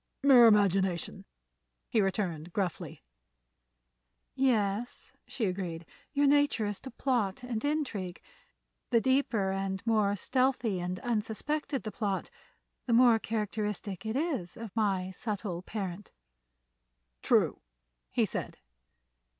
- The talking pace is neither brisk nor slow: No, slow, 110 wpm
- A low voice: No, high, 210 Hz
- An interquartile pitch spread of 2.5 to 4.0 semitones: No, average, 4.4 semitones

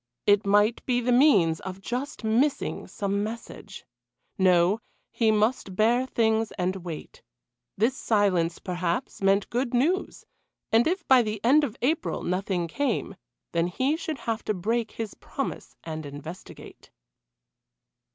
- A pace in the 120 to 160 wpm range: Yes, average, 140 wpm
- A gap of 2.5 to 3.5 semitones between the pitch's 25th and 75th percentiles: No, average, 4.7 semitones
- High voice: Yes, high, 215 Hz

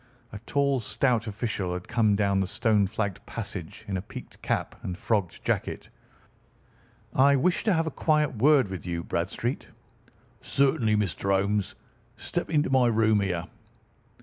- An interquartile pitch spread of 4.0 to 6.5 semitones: Yes, average, 5.2 semitones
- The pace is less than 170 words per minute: Yes, average, 150 wpm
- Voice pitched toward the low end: Yes, low, 110 Hz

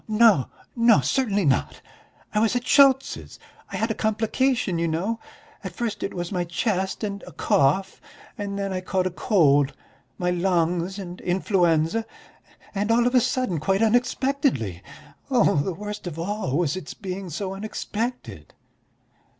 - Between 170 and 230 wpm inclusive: No, average, 155 wpm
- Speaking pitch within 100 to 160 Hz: No, high, 195 Hz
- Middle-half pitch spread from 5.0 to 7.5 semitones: No, average, 4.4 semitones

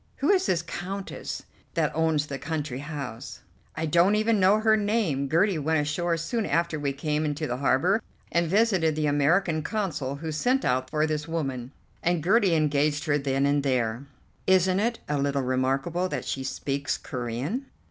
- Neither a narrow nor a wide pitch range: Yes, average, 4.7 semitones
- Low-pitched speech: No, medium, 155 Hz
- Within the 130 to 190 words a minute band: Yes, average, 175 wpm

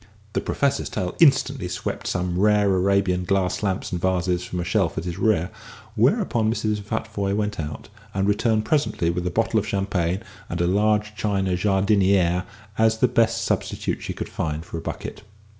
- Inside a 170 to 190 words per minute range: Yes, average, 175 wpm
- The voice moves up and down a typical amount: Yes, average, 3.1 semitones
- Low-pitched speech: Yes, low, 100 Hz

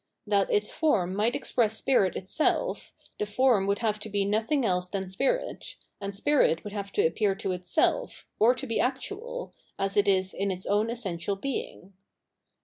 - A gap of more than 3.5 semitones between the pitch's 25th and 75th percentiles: Yes, average, 4.2 semitones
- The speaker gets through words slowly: No, average, 175 wpm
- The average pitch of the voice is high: Yes, high, 205 Hz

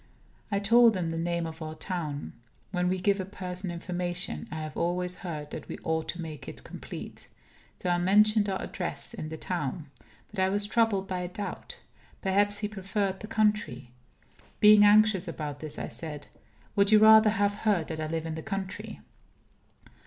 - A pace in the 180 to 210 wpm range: Yes, average, 185 wpm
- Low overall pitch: No, medium, 185 Hz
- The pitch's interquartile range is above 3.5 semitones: Yes, average, 4.0 semitones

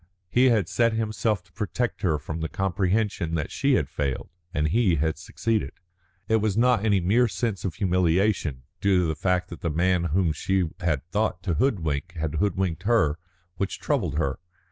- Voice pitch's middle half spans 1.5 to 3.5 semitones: No, average, 4.8 semitones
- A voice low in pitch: Yes, very low, 90 Hz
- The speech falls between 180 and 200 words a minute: Yes, average, 185 wpm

